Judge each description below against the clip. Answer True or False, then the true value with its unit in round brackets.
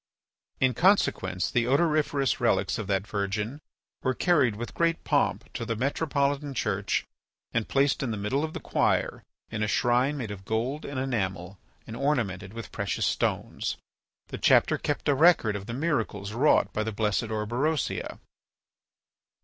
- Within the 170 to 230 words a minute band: False (155 wpm)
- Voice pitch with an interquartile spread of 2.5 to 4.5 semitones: False (5.1 semitones)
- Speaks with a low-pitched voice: True (120 Hz)